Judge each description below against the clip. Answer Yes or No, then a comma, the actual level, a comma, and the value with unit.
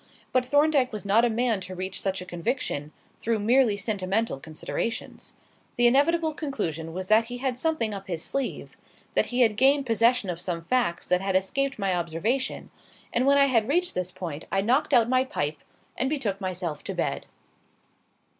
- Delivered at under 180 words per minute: No, average, 185 wpm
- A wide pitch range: Yes, wide, 5.7 semitones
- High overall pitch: Yes, high, 220 Hz